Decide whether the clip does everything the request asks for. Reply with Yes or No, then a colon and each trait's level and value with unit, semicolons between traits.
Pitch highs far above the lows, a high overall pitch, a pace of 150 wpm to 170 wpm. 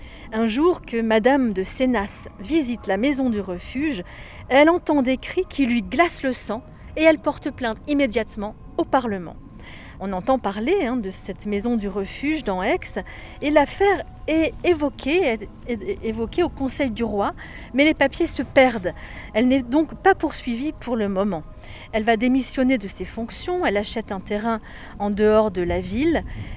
Yes: wide, 5.8 semitones; very high, 250 Hz; average, 165 wpm